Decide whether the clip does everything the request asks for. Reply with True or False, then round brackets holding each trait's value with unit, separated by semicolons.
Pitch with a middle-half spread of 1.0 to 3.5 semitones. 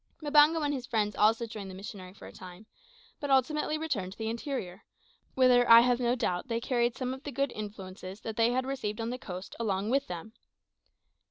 False (4.2 semitones)